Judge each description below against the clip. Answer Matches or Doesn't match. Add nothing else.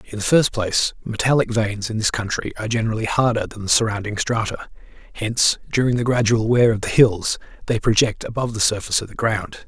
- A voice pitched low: Matches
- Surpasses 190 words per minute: Matches